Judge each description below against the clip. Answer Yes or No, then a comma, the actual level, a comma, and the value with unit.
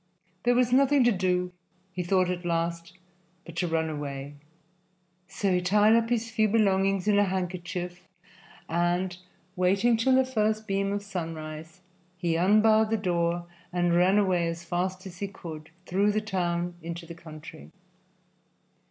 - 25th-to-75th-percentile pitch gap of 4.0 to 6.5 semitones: No, average, 3.4 semitones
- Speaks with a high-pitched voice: No, medium, 180 Hz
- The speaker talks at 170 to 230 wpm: No, average, 155 wpm